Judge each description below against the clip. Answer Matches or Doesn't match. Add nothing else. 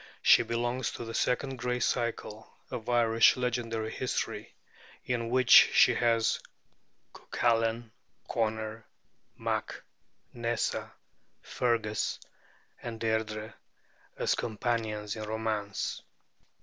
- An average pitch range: Doesn't match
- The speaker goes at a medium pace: Doesn't match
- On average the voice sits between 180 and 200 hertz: Doesn't match